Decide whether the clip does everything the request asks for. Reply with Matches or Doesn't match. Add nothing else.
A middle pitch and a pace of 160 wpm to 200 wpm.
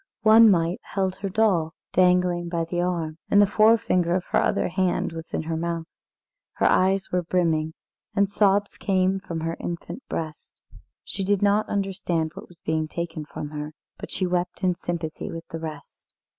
Matches